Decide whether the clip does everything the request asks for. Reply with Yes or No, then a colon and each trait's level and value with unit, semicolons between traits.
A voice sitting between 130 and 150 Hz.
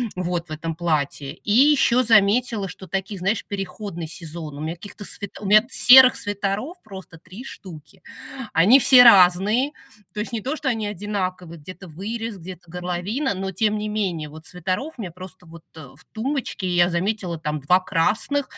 No: high, 190 Hz